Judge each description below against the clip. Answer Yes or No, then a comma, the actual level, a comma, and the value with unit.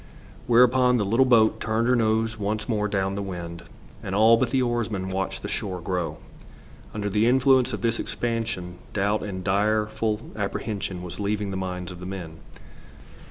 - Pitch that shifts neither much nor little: Yes, average, 3.3 semitones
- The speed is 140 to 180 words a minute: Yes, average, 170 wpm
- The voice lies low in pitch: Yes, low, 105 Hz